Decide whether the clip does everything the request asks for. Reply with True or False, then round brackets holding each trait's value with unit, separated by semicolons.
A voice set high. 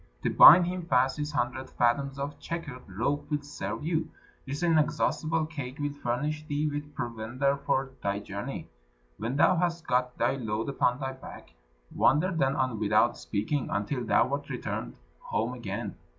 False (140 Hz)